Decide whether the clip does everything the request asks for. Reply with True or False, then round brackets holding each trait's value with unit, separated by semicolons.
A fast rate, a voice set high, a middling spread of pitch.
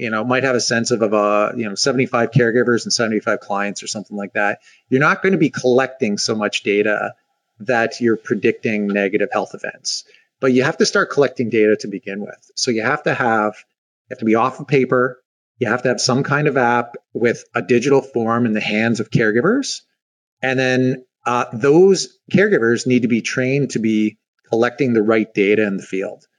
False (210 wpm; 120 Hz; 3.1 semitones)